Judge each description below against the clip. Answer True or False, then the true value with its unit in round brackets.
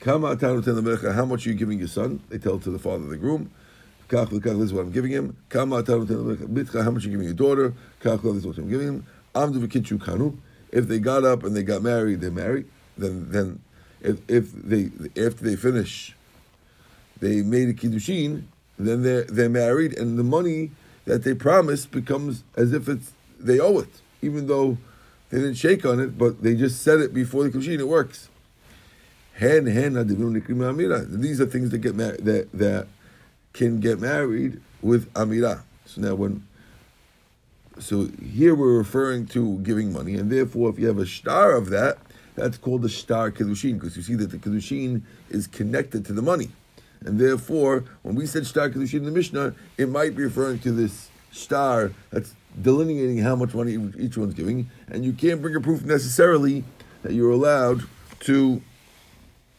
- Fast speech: False (175 wpm)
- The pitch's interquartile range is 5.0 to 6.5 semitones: False (3.6 semitones)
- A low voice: True (120 Hz)